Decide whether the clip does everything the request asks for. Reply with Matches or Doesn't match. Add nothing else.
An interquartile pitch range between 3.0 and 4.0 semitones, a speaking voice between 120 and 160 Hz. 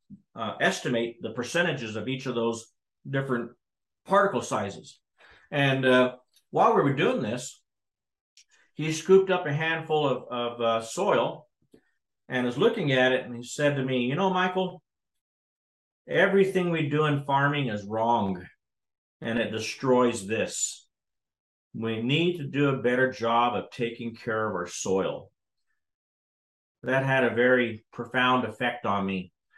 Matches